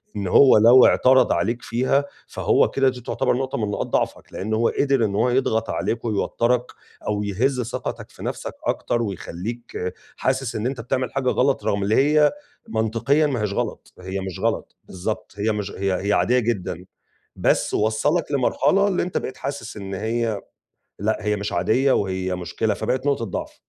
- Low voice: Yes, low, 115 Hz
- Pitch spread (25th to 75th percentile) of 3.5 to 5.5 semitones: Yes, average, 4.2 semitones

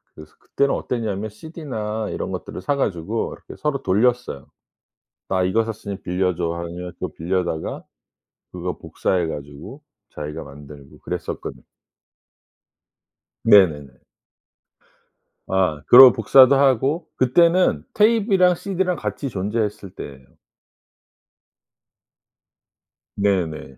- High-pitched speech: No, low, 100 Hz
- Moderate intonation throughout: No, wide, 7.7 semitones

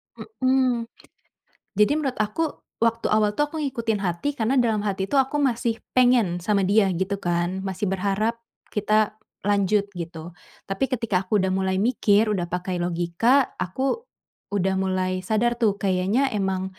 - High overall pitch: Yes, high, 205 Hz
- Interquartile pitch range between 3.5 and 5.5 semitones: Yes, average, 4.0 semitones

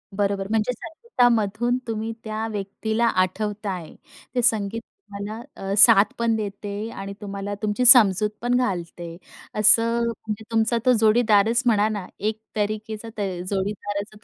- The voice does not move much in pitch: Yes, narrow, 2.1 semitones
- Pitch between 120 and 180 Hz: No, high, 215 Hz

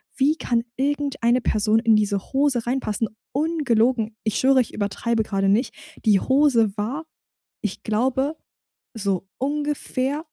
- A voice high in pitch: Yes, high, 240 Hz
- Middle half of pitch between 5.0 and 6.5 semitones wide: No, average, 4.3 semitones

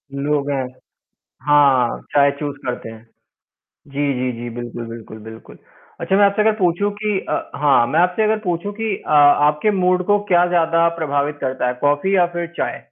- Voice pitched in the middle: Yes, medium, 150 Hz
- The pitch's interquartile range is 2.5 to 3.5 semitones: No, average, 4.8 semitones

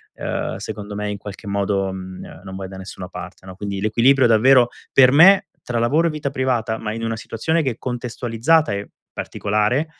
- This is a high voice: No, low, 110 Hz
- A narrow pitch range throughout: No, average, 4.6 semitones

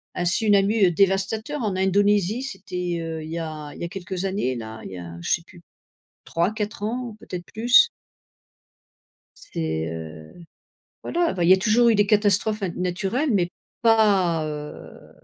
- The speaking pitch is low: No, high, 190 Hz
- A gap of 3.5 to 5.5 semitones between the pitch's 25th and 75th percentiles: Yes, average, 4.3 semitones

